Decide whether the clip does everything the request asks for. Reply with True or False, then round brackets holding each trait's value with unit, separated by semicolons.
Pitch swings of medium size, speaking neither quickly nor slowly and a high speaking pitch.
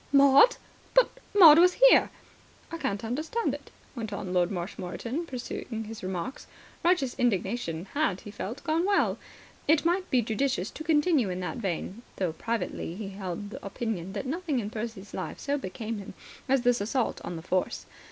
False (7.1 semitones; 170 wpm; 230 Hz)